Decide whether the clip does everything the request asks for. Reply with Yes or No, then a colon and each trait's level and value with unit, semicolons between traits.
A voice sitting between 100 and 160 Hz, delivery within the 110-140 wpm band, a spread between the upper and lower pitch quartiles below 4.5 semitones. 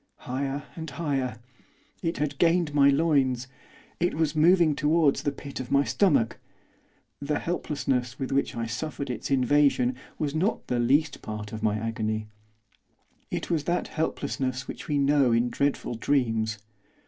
No: medium, 140 Hz; average, 150 wpm; average, 3.6 semitones